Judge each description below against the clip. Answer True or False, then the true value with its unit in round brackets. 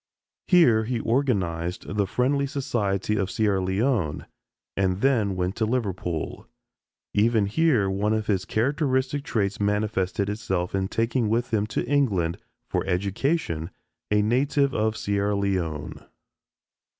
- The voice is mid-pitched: False (105 Hz)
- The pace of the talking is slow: True (125 wpm)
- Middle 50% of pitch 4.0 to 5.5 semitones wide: True (4.3 semitones)